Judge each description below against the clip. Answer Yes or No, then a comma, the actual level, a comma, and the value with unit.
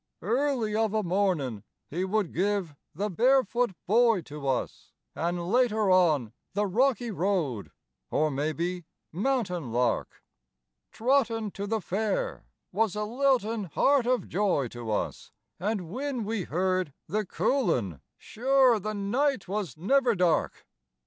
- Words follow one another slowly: Yes, slow, 130 wpm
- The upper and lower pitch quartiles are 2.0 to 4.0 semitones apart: No, average, 5.1 semitones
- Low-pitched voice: No, high, 205 Hz